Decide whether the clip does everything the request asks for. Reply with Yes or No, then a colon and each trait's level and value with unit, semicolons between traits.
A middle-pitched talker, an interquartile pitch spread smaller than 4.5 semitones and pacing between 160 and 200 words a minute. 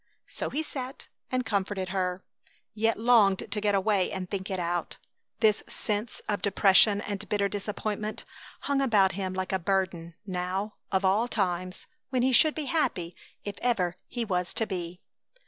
No: high, 200 Hz; average, 3.0 semitones; average, 165 wpm